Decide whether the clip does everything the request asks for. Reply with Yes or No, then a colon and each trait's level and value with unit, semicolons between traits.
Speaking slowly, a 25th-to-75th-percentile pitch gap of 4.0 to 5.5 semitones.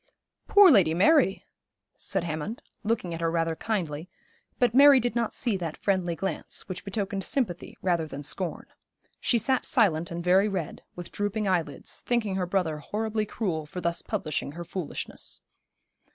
No: average, 160 wpm; average, 4.5 semitones